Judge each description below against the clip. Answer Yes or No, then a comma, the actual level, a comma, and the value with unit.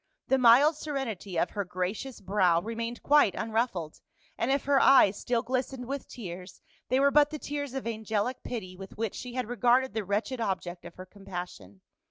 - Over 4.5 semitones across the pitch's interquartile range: Yes, wide, 5.6 semitones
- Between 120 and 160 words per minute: No, average, 185 wpm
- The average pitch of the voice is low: No, high, 230 Hz